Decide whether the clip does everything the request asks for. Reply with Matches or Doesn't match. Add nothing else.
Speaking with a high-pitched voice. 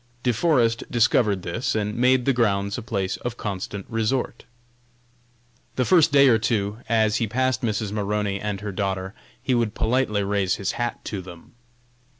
Doesn't match